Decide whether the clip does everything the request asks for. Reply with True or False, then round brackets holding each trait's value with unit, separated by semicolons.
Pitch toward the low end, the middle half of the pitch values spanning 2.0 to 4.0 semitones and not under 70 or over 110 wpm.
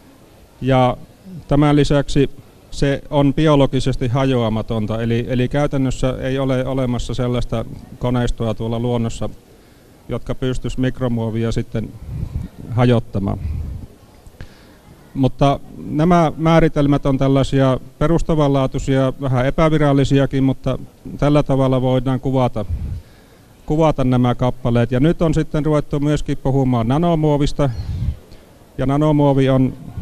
True (130 Hz; 3.0 semitones; 100 wpm)